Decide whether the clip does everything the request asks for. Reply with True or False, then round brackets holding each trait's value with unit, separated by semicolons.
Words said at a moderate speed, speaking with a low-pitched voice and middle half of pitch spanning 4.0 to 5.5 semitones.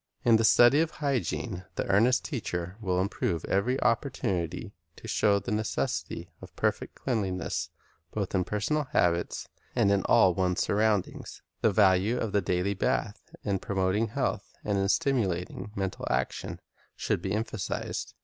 False (150 wpm; 100 Hz; 3.3 semitones)